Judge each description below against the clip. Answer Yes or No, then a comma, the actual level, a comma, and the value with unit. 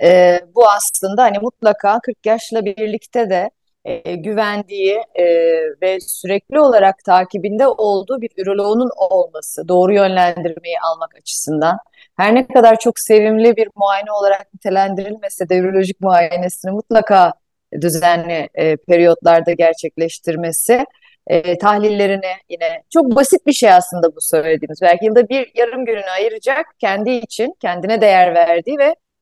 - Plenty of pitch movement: No, average, 4.8 semitones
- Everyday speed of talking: Yes, average, 130 wpm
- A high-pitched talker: Yes, high, 200 Hz